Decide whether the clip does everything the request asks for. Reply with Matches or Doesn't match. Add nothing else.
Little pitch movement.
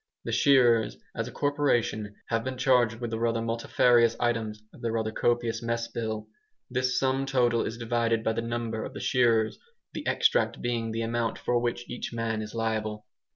Matches